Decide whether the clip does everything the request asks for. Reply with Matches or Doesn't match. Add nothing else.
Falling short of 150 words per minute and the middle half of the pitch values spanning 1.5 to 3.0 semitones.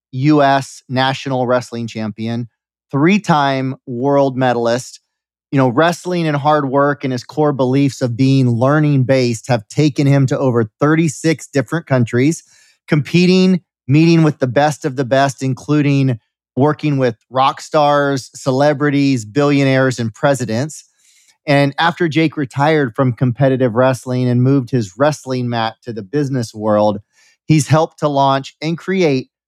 Matches